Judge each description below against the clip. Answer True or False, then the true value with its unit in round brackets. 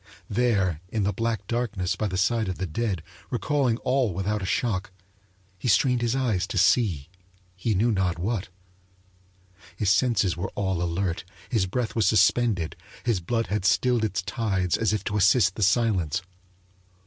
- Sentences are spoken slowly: False (165 wpm)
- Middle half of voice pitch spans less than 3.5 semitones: False (3.9 semitones)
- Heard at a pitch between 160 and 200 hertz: False (105 Hz)